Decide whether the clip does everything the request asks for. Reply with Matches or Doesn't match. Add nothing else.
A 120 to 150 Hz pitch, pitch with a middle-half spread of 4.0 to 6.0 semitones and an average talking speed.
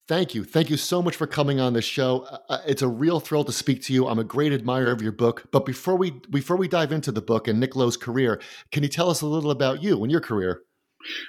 Doesn't match